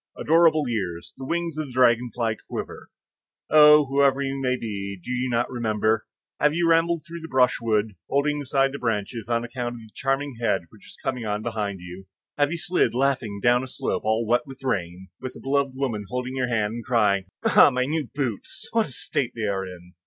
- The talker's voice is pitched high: No, low, 125 Hz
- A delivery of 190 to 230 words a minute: Yes, fast, 205 wpm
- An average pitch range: Yes, average, 4.2 semitones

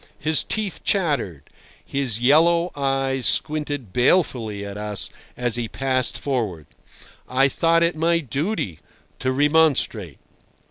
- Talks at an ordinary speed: No, slow, 120 wpm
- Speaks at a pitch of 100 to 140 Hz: Yes, low, 135 Hz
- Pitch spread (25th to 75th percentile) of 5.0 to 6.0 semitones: Yes, wide, 5.6 semitones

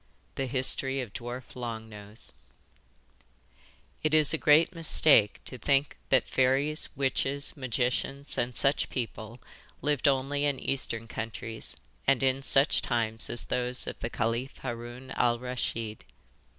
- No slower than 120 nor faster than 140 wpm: Yes, slow, 135 wpm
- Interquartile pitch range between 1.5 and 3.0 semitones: Yes, average, 2.7 semitones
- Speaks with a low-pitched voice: Yes, low, 130 Hz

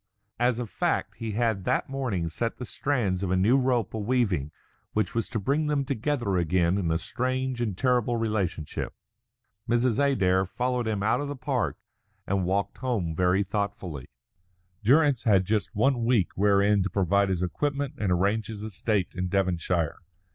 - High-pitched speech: No, low, 105 Hz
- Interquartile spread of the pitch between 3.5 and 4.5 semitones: No, average, 5.0 semitones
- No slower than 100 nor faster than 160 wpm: No, average, 170 wpm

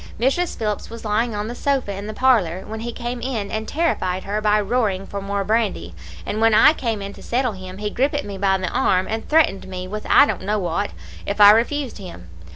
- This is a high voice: Yes, high, 210 Hz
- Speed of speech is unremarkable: No, fast, 230 wpm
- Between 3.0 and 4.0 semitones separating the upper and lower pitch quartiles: Yes, average, 3.3 semitones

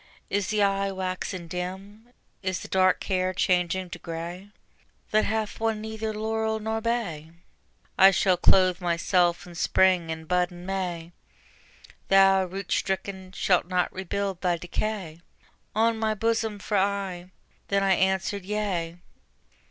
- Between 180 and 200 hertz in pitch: Yes, high, 190 Hz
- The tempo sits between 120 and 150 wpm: Yes, average, 140 wpm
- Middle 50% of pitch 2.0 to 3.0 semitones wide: Yes, narrow, 2.5 semitones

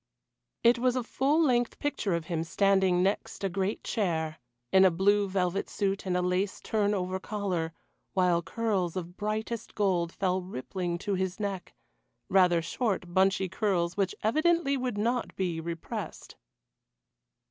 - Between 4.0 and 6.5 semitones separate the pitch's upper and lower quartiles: No, average, 2.9 semitones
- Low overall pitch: No, high, 190 Hz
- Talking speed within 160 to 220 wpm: No, average, 150 wpm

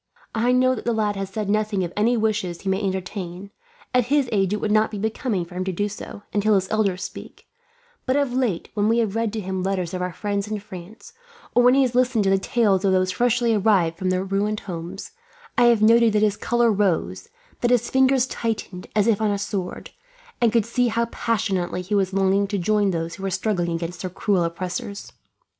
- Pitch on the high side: Yes, high, 205 Hz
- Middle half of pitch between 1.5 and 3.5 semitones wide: Yes, average, 3.2 semitones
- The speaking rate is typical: No, fast, 225 wpm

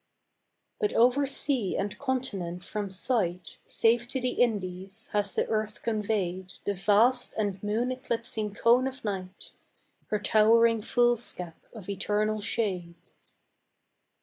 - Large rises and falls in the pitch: No, average, 3.5 semitones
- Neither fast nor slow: No, slow, 120 wpm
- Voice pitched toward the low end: No, high, 215 Hz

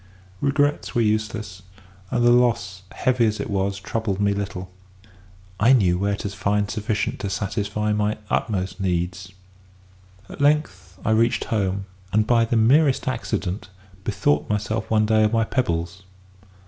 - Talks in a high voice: No, low, 105 Hz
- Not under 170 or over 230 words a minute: No, average, 150 wpm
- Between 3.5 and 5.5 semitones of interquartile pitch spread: No, average, 2.7 semitones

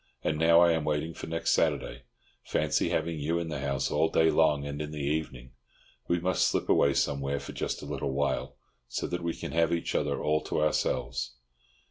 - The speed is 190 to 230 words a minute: Yes, fast, 205 wpm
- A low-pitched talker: Yes, very low, 75 Hz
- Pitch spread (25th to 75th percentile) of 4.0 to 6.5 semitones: No, narrow, 2.5 semitones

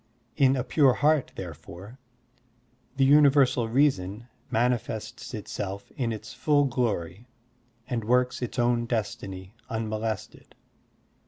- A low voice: Yes, low, 120 Hz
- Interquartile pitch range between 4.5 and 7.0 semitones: No, average, 3.8 semitones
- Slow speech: Yes, slow, 105 wpm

